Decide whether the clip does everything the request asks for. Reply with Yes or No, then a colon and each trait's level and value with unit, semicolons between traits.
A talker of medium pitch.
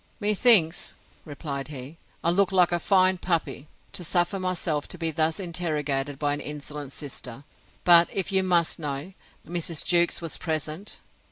Yes: medium, 165 Hz